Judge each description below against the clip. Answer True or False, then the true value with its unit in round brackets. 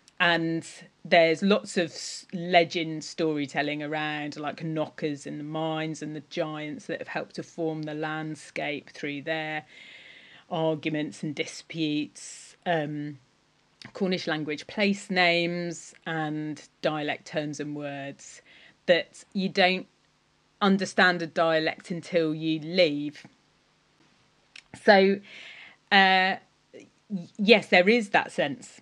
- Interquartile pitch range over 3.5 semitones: False (2.9 semitones)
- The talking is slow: True (110 wpm)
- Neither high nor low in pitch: True (160 Hz)